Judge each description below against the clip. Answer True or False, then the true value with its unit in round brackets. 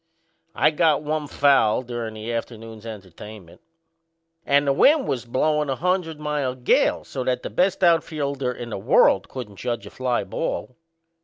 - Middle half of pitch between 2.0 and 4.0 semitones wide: False (4.6 semitones)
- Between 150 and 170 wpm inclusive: True (160 wpm)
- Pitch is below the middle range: True (130 Hz)